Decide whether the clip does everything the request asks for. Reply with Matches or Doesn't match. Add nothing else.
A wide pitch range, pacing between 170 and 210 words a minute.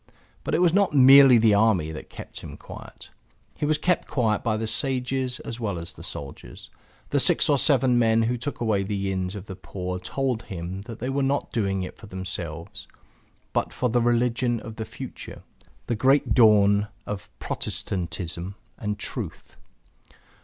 Doesn't match